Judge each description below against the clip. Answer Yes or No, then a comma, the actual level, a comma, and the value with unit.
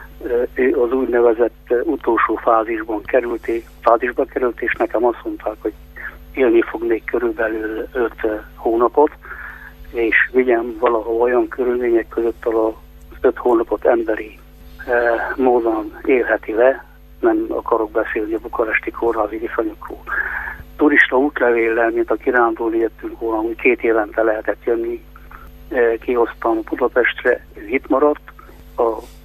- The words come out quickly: No, average, 115 wpm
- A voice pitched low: Yes, low, 120 Hz